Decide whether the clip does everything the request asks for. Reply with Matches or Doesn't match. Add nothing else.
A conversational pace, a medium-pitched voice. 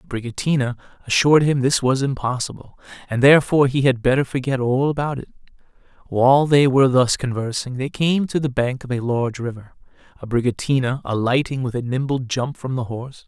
Doesn't match